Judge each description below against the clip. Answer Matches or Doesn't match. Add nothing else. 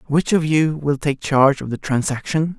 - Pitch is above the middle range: Doesn't match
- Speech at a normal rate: Doesn't match